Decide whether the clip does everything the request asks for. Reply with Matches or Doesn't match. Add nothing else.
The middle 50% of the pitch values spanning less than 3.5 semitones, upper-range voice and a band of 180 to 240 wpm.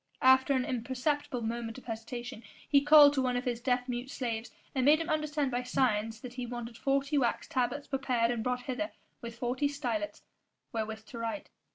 Matches